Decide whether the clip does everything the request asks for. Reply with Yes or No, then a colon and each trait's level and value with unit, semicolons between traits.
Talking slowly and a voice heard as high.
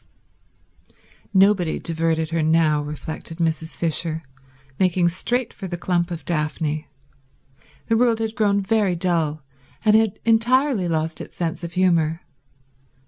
No: slow, 130 wpm; medium, 170 Hz